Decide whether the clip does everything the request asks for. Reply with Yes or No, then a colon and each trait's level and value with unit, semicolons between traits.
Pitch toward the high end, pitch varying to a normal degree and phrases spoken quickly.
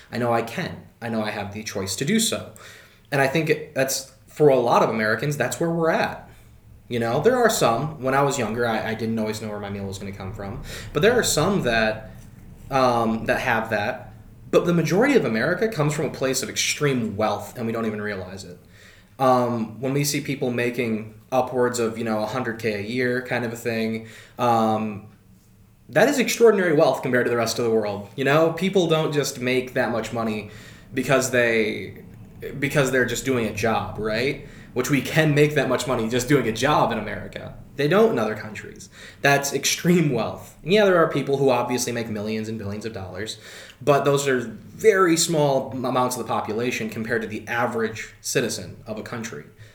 No: low, 120 Hz; average, 4.2 semitones; fast, 210 wpm